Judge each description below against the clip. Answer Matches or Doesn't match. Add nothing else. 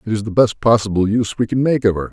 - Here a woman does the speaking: Doesn't match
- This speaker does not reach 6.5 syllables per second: Doesn't match